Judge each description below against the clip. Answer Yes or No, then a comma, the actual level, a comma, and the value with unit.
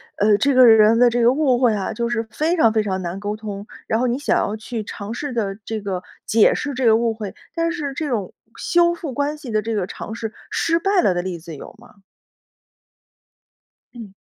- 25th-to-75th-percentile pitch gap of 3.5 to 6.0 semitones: Yes, average, 4.5 semitones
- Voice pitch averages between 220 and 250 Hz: Yes, high, 230 Hz